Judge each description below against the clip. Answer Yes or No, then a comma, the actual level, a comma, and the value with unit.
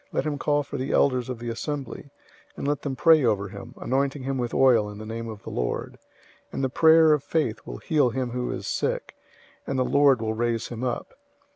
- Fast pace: Yes, fast, 230 wpm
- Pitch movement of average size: Yes, average, 3.6 semitones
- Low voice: Yes, low, 130 Hz